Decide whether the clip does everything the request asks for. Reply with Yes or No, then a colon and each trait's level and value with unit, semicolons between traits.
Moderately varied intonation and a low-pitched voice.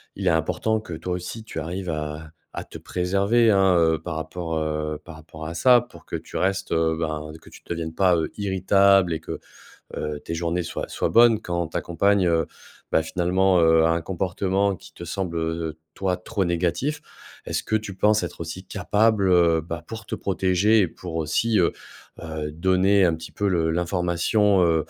Yes: average, 3.1 semitones; very low, 90 Hz